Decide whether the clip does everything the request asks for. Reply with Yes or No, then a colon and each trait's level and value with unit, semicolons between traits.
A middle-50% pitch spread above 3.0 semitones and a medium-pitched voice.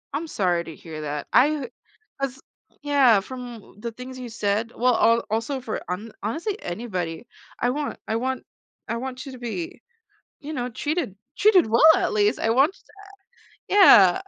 No: average, 4.7 semitones; high, 240 Hz